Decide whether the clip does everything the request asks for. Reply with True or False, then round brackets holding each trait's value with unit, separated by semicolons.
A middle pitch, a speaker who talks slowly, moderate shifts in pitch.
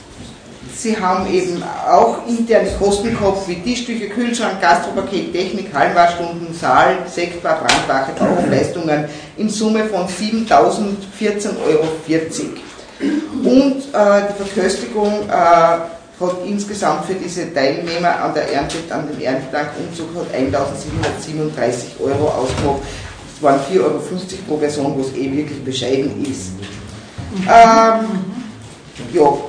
False (175 Hz; 110 wpm; 5.7 semitones)